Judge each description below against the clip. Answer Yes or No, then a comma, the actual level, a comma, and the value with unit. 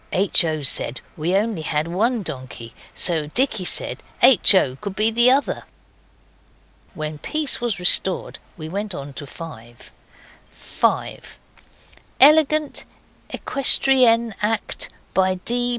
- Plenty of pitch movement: Yes, wide, 7.4 semitones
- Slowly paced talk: Yes, slow, 120 wpm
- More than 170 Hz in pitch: Yes, high, 190 Hz